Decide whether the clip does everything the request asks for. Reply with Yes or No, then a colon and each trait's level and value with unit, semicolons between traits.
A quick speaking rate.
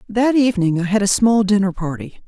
Yes: fast, 210 wpm